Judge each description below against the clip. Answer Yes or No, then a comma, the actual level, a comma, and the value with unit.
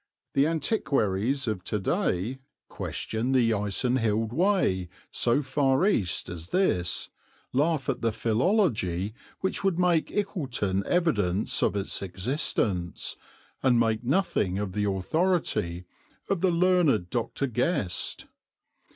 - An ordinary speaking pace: No, slow, 115 wpm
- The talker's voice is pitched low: Yes, low, 120 Hz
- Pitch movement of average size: No, wide, 8.6 semitones